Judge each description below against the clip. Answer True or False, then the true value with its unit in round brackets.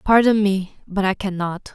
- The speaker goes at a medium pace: True (170 wpm)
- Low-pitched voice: False (195 Hz)